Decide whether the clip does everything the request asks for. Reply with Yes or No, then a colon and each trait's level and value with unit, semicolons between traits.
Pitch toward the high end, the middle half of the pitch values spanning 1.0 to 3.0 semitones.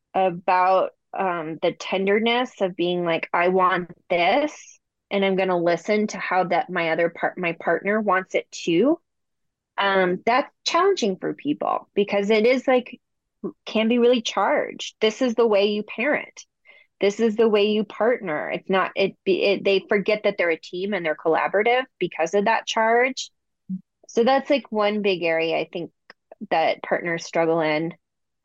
No: high, 200 Hz; average, 4.7 semitones